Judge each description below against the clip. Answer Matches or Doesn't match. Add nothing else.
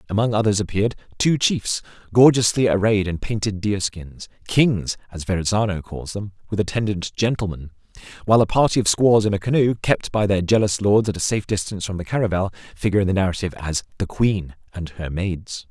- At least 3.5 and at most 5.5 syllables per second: Doesn't match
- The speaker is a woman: Doesn't match